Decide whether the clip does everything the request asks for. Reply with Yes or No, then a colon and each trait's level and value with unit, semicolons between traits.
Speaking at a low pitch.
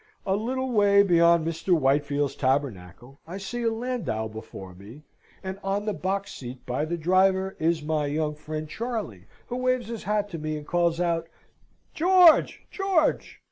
No: medium, 170 Hz